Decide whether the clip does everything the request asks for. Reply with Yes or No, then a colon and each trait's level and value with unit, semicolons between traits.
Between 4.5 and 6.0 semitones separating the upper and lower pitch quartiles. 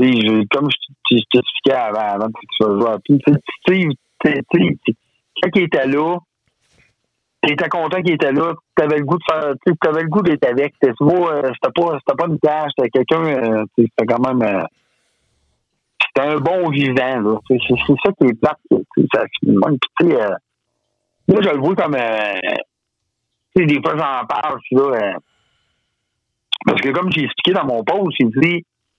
Yes: average, 5.1 semitones